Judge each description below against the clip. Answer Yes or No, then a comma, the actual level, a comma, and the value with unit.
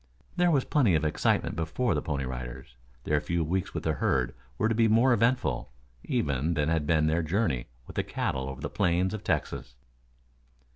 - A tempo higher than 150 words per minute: Yes, average, 190 wpm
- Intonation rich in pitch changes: Yes, wide, 7.2 semitones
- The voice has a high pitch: No, very low, 80 Hz